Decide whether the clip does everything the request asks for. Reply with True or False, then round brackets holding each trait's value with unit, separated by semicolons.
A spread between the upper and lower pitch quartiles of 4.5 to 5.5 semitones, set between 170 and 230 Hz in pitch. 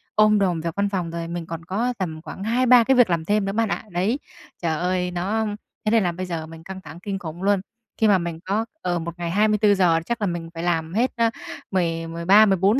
False (3.9 semitones; 185 Hz)